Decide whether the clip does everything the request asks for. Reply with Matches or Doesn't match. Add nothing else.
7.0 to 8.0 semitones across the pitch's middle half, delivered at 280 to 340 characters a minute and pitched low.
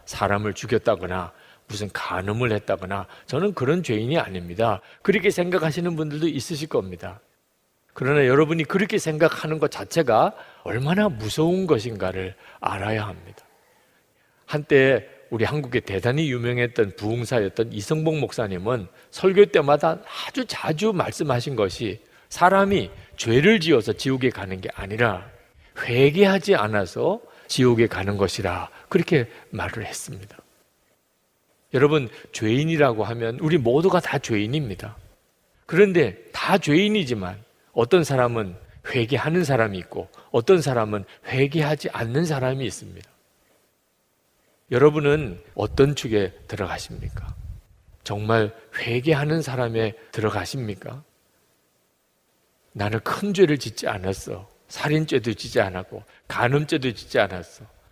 Matches